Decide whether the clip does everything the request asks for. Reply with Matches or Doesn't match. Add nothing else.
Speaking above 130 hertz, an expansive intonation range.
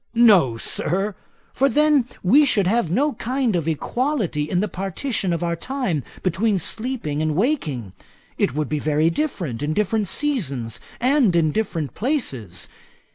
Matches